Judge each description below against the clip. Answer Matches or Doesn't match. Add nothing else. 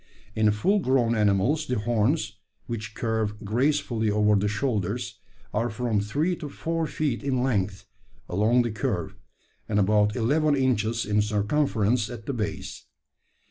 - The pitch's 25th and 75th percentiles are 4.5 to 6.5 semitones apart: Doesn't match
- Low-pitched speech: Matches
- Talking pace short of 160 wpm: Matches